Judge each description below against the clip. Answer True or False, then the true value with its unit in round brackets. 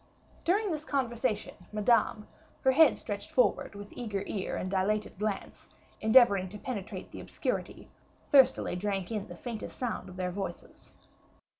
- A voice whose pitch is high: True (215 Hz)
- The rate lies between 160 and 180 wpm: False (145 wpm)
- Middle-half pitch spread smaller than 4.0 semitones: False (4.3 semitones)